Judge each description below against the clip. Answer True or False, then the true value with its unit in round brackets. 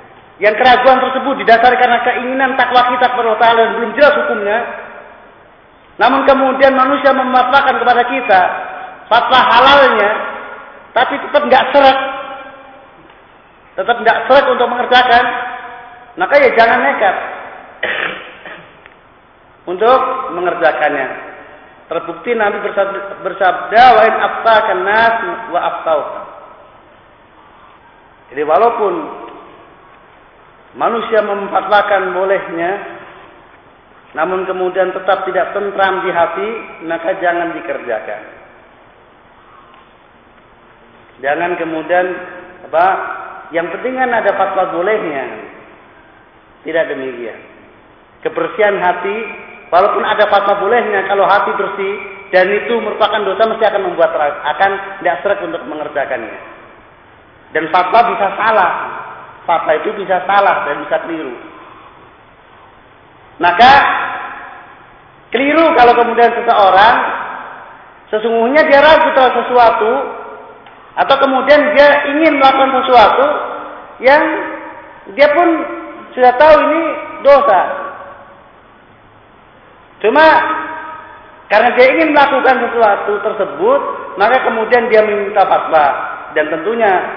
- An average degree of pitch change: False (5.9 semitones)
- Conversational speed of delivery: True (95 wpm)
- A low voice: False (230 Hz)